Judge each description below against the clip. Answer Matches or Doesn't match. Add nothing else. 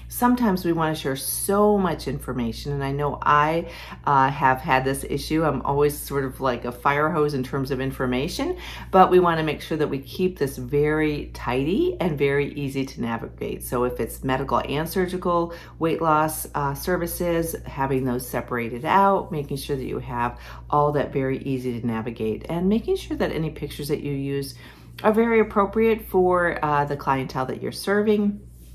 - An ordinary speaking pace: Matches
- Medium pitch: Matches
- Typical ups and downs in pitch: Matches